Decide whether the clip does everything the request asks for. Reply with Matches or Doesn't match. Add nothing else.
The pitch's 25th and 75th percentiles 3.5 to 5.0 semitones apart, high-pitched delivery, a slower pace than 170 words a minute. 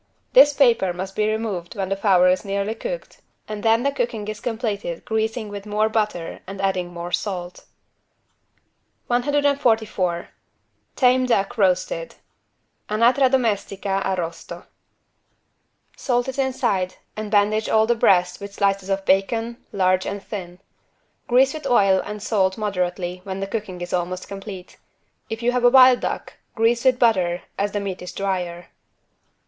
Matches